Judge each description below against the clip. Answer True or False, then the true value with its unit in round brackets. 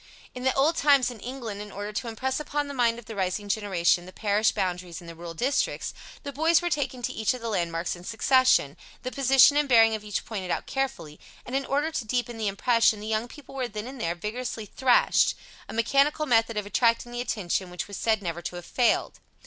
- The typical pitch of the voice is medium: False (230 Hz)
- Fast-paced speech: True (230 wpm)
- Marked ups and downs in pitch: False (4.5 semitones)